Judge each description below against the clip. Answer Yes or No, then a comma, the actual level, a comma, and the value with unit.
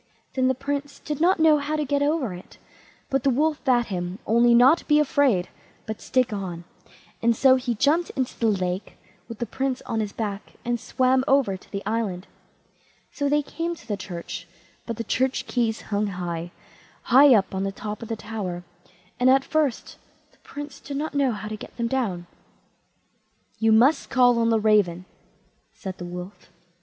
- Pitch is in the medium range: No, high, 235 Hz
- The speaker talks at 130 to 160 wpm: No, average, 190 wpm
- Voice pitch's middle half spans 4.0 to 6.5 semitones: Yes, average, 5.2 semitones